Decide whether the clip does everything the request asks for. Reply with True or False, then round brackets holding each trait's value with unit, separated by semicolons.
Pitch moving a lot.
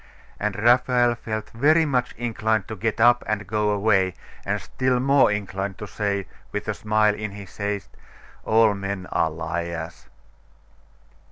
False (2.8 semitones)